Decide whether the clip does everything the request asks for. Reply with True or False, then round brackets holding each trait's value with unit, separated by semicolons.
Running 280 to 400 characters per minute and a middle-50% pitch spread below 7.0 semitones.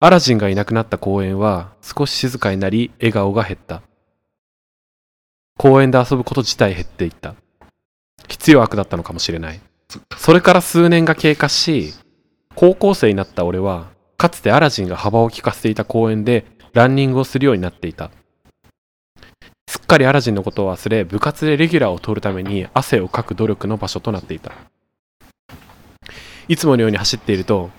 True (355 characters per minute; 5.6 semitones)